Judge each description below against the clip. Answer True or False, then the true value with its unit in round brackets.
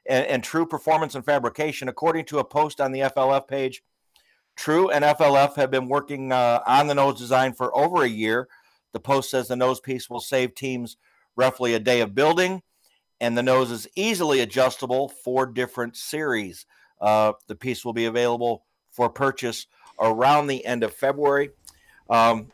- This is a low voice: True (130 Hz)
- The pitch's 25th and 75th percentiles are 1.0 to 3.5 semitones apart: True (2.8 semitones)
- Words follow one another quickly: False (175 wpm)